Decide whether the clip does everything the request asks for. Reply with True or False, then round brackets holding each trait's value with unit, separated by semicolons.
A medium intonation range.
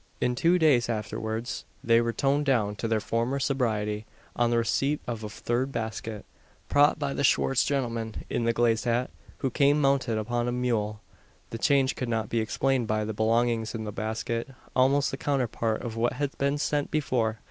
True (3.3 semitones)